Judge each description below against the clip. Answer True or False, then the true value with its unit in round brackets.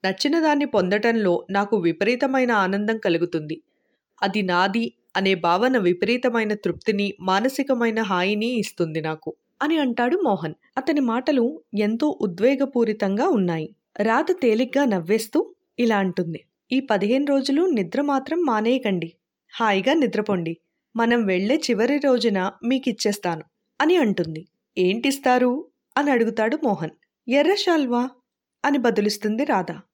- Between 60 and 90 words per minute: False (105 wpm)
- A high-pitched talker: True (225 Hz)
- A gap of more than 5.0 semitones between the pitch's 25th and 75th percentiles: True (5.5 semitones)